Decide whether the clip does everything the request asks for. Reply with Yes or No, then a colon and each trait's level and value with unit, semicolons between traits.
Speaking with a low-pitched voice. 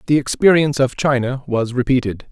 Yes: low, 130 Hz